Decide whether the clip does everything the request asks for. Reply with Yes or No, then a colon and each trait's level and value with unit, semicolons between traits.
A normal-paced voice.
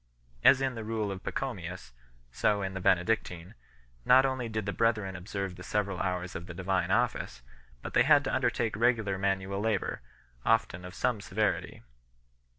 Yes: average, 170 wpm